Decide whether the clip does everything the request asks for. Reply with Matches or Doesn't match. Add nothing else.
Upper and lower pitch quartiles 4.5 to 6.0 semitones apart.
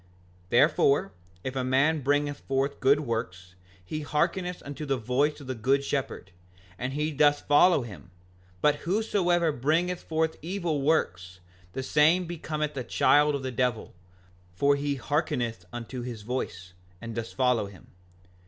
Doesn't match